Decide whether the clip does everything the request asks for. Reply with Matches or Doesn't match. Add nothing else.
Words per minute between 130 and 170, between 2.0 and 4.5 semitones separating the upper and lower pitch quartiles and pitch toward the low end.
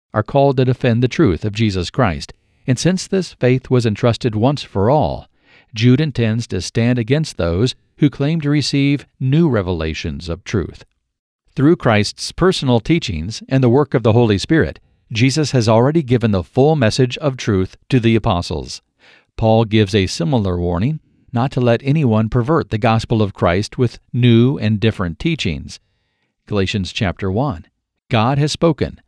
Doesn't match